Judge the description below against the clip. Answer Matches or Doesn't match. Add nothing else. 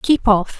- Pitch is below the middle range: Doesn't match